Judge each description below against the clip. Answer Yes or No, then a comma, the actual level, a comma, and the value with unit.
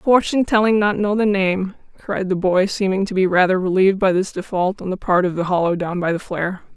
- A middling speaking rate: No, fast, 240 wpm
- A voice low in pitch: No, high, 190 Hz